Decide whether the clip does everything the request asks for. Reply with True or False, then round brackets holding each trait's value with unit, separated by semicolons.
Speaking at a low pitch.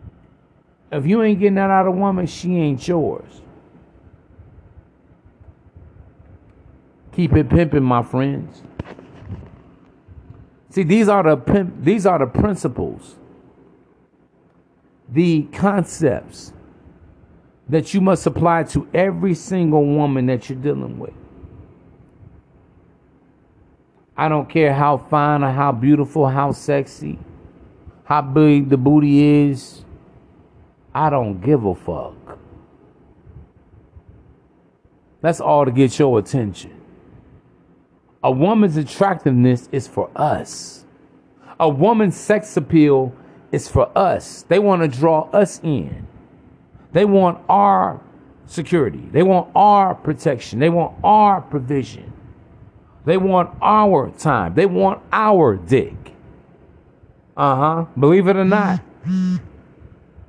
False (150 Hz)